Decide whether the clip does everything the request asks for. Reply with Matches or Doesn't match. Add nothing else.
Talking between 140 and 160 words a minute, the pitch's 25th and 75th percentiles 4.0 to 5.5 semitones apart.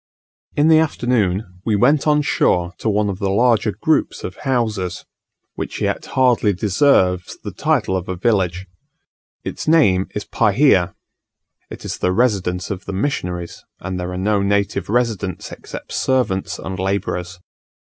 Matches